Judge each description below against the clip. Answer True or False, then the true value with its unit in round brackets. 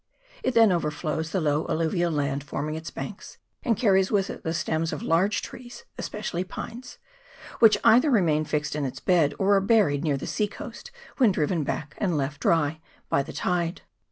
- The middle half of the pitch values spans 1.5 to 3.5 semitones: False (4.9 semitones)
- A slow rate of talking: False (185 wpm)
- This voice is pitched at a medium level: True (170 Hz)